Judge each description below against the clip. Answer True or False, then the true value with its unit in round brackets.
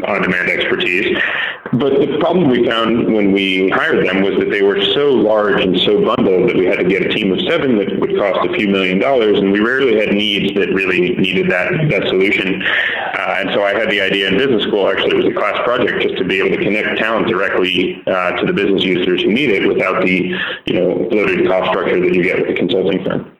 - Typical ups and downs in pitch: False (5.8 semitones)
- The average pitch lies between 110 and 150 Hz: False (100 Hz)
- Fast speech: True (240 wpm)